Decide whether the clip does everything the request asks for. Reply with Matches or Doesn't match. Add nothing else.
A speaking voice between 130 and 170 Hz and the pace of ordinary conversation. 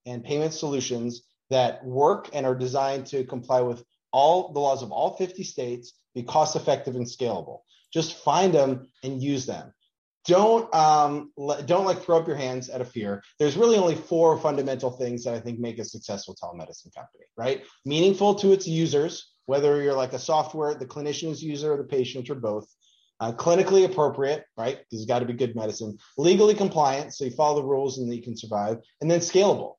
Matches